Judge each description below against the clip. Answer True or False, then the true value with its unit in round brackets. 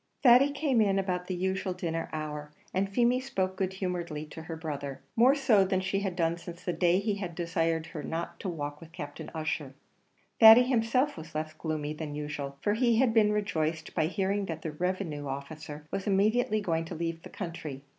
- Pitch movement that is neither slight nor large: True (4.3 semitones)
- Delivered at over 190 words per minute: True (200 wpm)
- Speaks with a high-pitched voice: False (175 Hz)